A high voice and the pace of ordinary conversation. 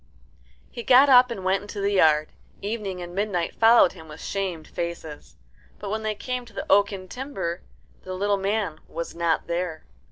Yes: high, 195 Hz; average, 180 wpm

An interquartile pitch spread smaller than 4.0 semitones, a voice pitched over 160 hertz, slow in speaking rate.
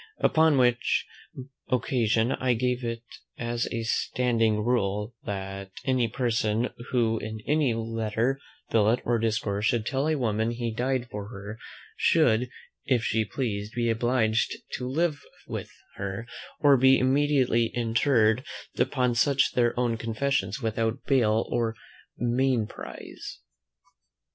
No: narrow, 2.5 semitones; low, 115 Hz; slow, 125 wpm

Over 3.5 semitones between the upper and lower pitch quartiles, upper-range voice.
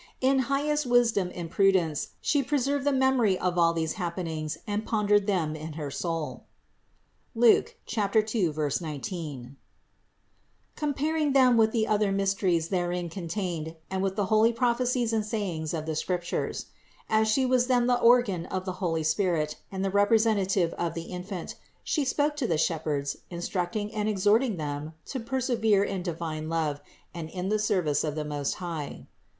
Yes: wide, 5.6 semitones; high, 195 Hz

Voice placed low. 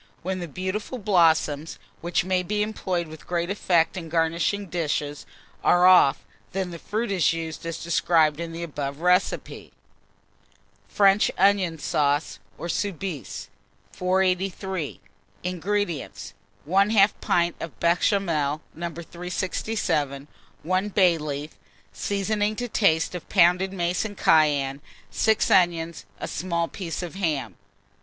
No: medium, 175 Hz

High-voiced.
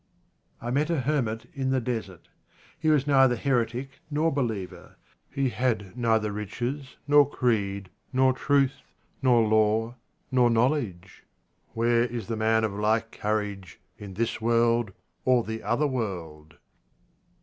No: low, 115 Hz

